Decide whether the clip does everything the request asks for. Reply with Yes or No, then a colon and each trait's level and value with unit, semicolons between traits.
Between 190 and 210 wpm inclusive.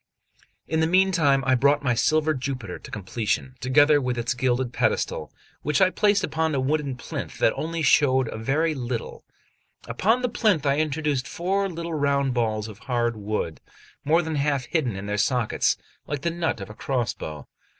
No: average, 180 wpm